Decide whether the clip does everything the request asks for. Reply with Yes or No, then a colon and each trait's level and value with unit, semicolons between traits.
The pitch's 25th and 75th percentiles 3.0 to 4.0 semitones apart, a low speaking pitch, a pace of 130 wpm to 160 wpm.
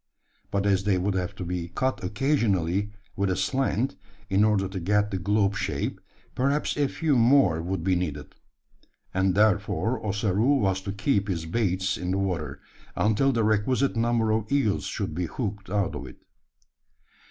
No: average, 3.5 semitones; low, 100 Hz; average, 170 wpm